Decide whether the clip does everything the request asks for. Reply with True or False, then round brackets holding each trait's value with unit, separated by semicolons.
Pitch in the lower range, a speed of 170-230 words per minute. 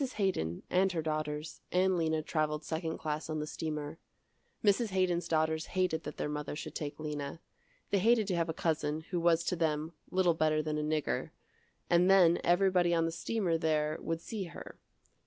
False (160 Hz; 185 wpm)